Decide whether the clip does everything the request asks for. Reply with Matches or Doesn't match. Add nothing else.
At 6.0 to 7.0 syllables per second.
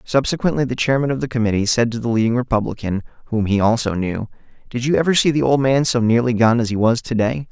Matches